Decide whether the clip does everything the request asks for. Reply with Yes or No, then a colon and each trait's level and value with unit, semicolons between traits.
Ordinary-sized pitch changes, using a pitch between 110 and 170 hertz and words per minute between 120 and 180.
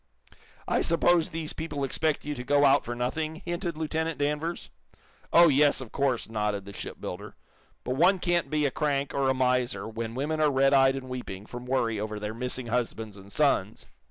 No: average, 4.4 semitones; low, 135 Hz; average, 190 wpm